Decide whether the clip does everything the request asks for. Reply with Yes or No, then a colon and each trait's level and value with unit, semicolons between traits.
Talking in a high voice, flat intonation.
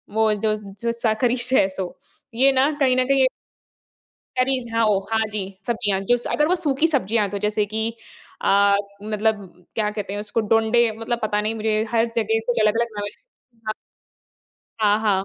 Yes: high, 220 Hz; narrow, 2.3 semitones